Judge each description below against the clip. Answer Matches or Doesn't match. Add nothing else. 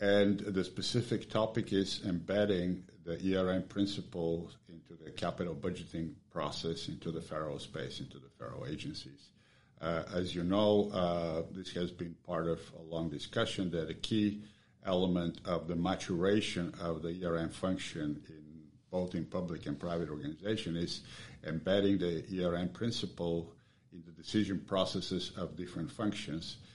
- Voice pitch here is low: Matches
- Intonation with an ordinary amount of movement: Matches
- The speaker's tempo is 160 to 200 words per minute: Doesn't match